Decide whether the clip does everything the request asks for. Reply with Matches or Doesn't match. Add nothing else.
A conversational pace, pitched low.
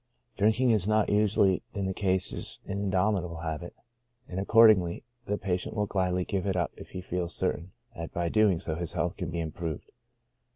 Matches